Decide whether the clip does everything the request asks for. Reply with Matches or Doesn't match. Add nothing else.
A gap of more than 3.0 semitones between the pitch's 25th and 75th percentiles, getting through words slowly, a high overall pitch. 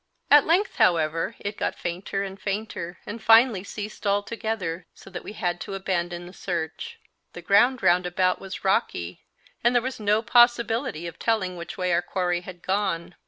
Doesn't match